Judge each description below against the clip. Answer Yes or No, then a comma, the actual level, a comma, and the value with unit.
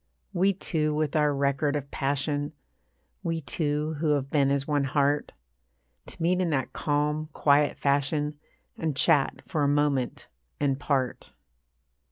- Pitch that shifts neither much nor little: No, narrow, 1.5 semitones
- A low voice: No, medium, 145 Hz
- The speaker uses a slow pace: No, average, 145 wpm